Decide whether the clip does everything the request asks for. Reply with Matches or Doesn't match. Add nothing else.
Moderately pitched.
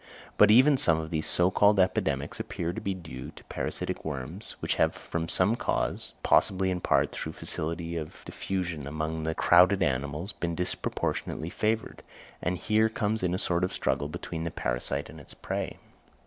Doesn't match